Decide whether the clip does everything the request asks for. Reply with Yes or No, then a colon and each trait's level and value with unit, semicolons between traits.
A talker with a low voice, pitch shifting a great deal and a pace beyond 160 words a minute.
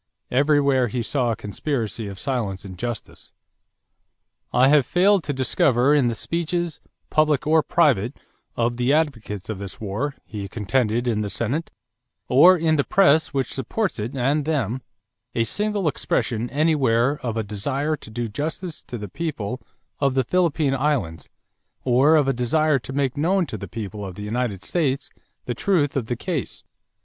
No: low, 130 Hz; average, 5.0 semitones; average, 170 wpm